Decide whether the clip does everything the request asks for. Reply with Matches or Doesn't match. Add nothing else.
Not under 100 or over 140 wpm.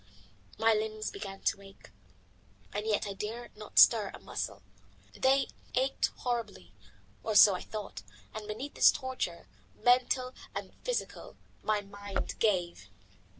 Matches